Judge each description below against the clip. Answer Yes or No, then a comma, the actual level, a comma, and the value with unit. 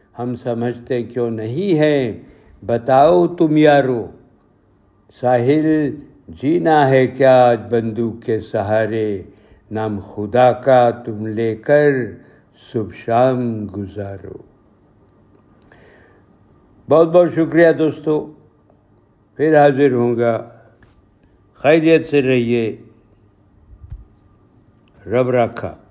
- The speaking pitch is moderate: No, low, 120 Hz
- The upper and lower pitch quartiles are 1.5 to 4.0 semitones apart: No, average, 4.5 semitones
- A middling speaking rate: No, slow, 90 wpm